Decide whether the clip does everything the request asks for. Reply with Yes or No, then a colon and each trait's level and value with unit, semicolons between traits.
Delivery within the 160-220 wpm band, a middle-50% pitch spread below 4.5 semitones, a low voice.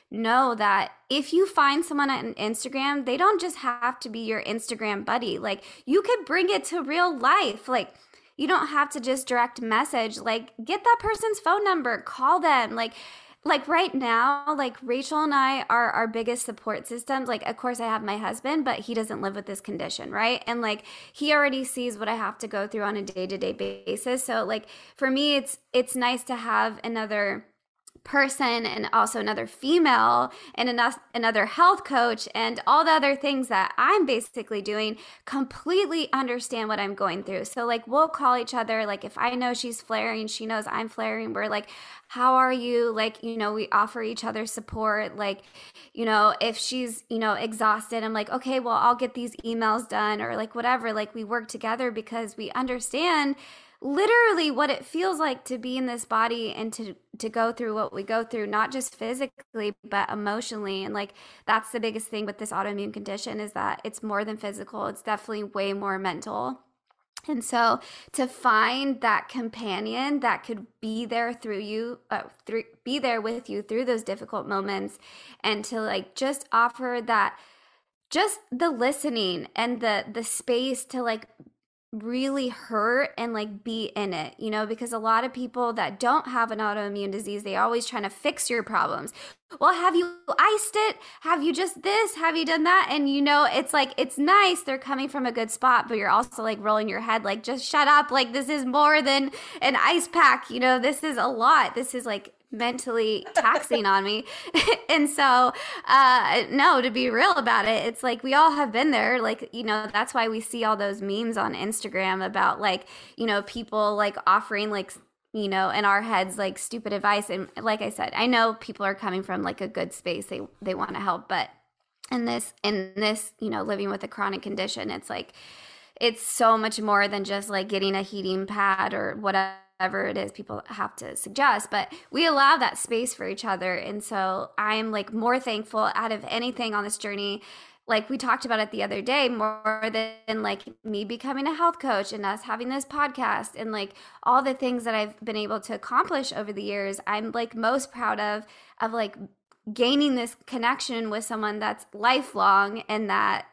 No: average, 200 wpm; average, 3.9 semitones; high, 230 Hz